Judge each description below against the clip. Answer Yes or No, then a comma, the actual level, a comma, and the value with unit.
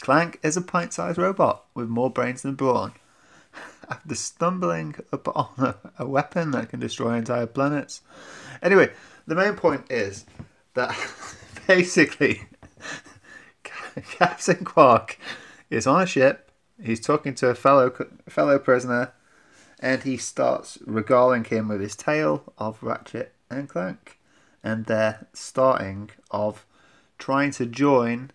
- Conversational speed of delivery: No, slow, 125 wpm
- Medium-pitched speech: No, low, 125 Hz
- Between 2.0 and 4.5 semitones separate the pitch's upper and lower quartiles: Yes, average, 3.7 semitones